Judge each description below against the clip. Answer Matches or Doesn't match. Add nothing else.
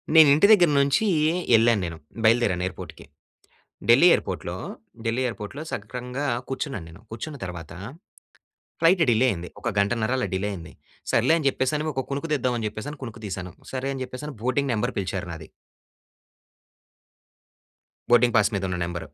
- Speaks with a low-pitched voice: Matches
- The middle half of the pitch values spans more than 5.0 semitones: Matches